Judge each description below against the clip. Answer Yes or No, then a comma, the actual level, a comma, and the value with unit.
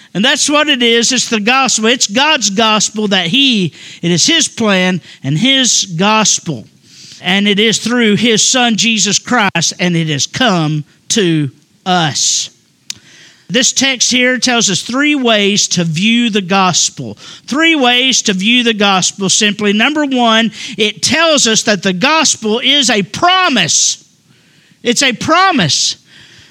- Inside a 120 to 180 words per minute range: Yes, average, 150 wpm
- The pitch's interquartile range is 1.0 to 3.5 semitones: No, average, 5.2 semitones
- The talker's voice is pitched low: No, high, 215 Hz